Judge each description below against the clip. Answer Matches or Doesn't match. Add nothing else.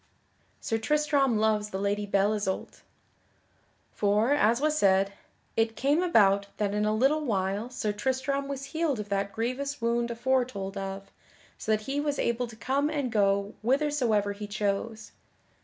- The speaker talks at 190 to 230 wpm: Doesn't match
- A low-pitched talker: Doesn't match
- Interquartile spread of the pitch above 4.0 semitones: Matches